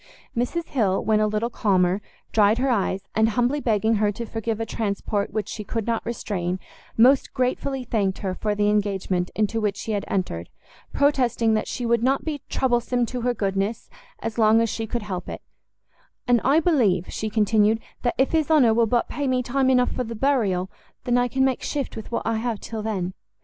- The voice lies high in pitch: Yes, high, 225 Hz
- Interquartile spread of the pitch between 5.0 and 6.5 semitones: No, average, 3.1 semitones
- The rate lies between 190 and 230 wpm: Yes, average, 200 wpm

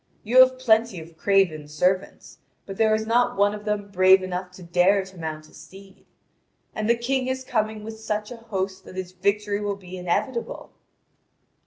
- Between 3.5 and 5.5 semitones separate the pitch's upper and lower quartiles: No, average, 2.9 semitones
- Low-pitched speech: No, high, 200 Hz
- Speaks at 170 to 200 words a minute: Yes, average, 185 wpm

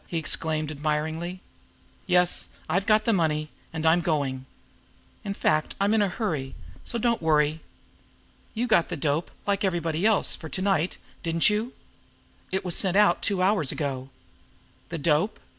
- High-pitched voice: No, medium, 170 Hz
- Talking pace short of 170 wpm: Yes, average, 160 wpm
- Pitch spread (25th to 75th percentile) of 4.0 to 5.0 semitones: Yes, average, 4.5 semitones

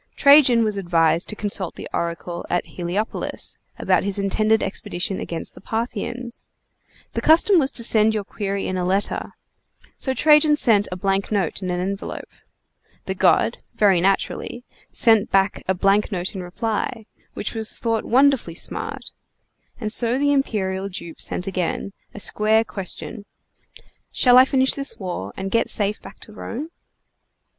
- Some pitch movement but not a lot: Yes, average, 3.7 semitones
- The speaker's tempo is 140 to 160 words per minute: Yes, average, 155 wpm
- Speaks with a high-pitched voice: Yes, high, 205 Hz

